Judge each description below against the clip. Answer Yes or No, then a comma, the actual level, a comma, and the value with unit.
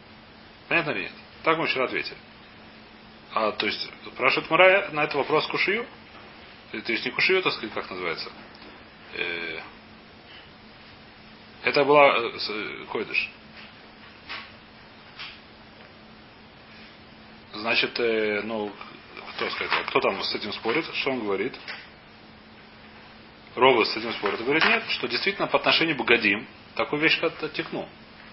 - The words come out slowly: No, average, 120 wpm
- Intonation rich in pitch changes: Yes, wide, 6.5 semitones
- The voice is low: No, medium, 150 Hz